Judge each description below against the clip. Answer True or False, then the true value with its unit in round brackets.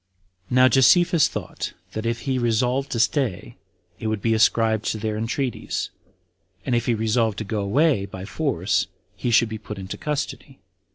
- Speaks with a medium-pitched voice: False (115 Hz)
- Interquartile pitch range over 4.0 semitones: False (3.1 semitones)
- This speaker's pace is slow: False (175 wpm)